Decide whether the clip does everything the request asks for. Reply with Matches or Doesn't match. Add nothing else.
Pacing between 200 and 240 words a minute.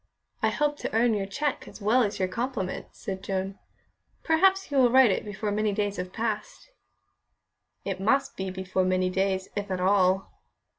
Doesn't match